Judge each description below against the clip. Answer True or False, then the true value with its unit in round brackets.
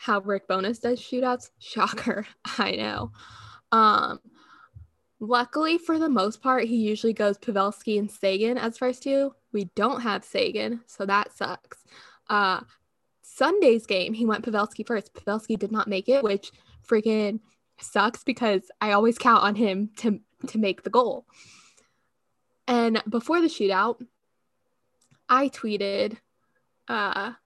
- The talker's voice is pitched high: True (225 Hz)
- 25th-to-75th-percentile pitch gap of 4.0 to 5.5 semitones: False (3.3 semitones)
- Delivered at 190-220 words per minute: False (140 wpm)